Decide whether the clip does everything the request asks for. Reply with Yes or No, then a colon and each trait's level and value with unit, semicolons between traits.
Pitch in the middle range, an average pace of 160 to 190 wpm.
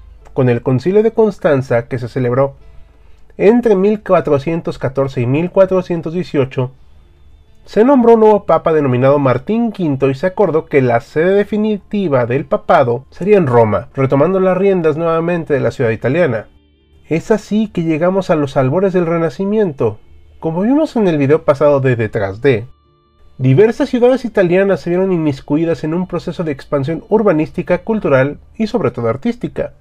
No: medium, 160 Hz; average, 150 wpm